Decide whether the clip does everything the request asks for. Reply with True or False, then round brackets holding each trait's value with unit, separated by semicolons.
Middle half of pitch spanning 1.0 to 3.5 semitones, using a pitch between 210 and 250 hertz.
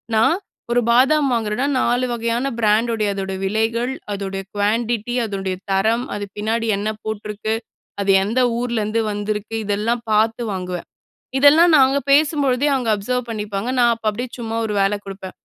True (2.8 semitones; 225 Hz)